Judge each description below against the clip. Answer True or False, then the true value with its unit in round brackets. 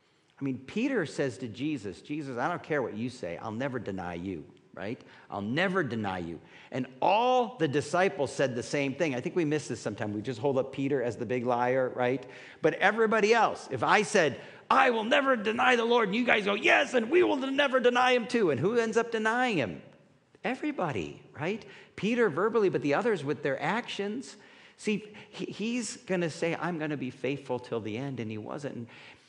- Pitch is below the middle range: False (160 Hz)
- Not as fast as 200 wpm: False (205 wpm)